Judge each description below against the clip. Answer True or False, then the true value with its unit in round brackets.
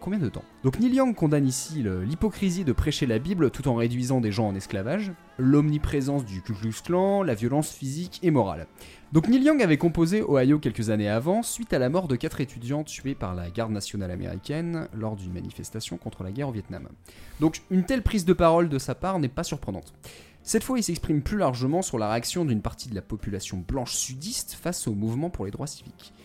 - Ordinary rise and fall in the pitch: False (7.4 semitones)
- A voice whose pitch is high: False (135 Hz)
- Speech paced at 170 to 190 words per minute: False (220 wpm)